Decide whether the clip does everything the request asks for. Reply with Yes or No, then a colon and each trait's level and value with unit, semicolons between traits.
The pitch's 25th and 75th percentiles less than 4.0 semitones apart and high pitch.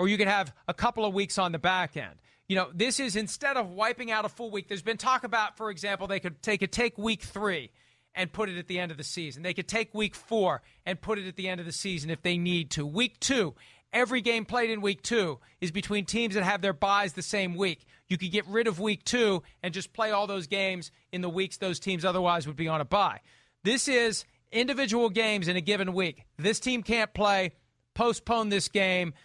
Yes: average, 3.5 semitones; high, 200 Hz